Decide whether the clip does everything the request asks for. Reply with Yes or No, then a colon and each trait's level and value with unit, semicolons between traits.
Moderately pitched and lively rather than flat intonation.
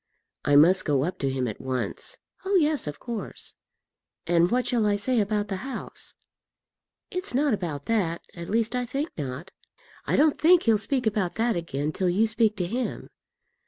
No: high, 210 Hz; wide, 6.7 semitones